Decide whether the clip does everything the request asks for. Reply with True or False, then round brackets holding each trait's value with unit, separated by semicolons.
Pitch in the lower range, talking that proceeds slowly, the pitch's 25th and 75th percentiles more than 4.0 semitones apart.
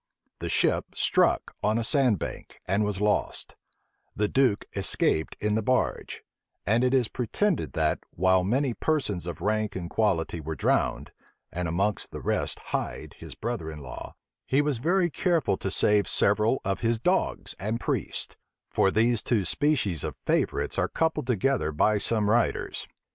False (105 Hz; 165 wpm; 4.9 semitones)